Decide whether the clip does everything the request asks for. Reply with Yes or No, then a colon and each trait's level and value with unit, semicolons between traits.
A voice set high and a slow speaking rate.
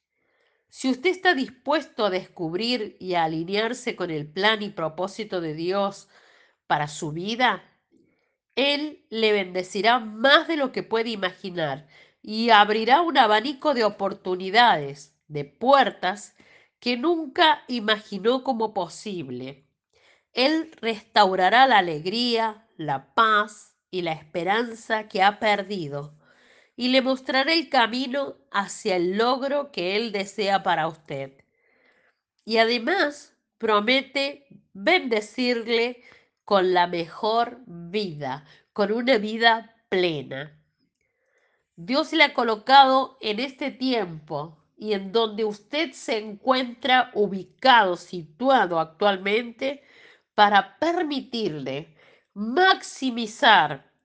Yes: high, 215 Hz; slow, 110 wpm